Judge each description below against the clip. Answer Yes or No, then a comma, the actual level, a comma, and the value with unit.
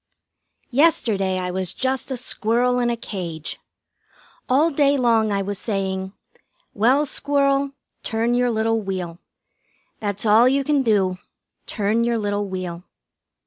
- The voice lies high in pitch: Yes, high, 225 Hz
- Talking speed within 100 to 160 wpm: Yes, slow, 135 wpm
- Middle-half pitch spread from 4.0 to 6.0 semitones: Yes, average, 4.7 semitones